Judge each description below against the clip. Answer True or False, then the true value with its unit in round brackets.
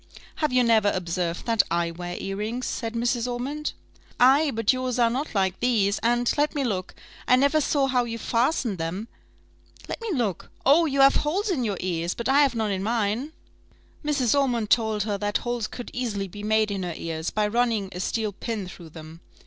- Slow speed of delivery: False (200 wpm)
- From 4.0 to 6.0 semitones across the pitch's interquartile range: True (4.4 semitones)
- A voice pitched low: False (230 Hz)